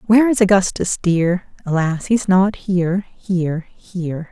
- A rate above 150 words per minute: No, average, 140 wpm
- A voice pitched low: No, medium, 185 Hz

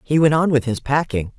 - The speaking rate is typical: No, fast, 260 wpm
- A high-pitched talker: No, medium, 140 Hz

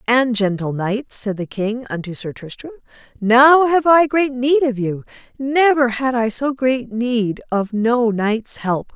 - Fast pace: No, average, 175 wpm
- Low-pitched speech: No, high, 240 Hz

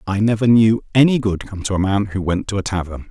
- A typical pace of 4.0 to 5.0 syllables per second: No, 5.9 syllables/s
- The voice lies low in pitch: Yes, low, 100 Hz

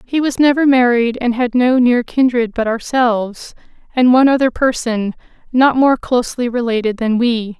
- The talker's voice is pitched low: No, high, 245 Hz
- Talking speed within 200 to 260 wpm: No, average, 165 wpm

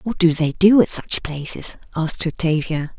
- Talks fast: No, average, 180 wpm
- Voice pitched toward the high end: No, medium, 170 Hz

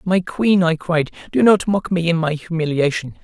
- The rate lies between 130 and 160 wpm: No, fast, 205 wpm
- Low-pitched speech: No, medium, 170 Hz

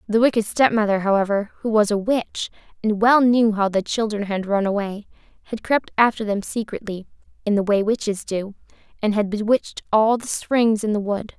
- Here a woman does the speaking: Yes, female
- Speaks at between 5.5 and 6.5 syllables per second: No, 5.2 syllables/s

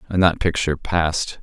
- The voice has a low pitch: Yes, very low, 85 Hz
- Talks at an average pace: Yes, average, 170 wpm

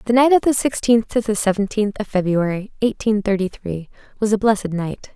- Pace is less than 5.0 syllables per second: No, 5.5 syllables/s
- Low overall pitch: No, high, 210 Hz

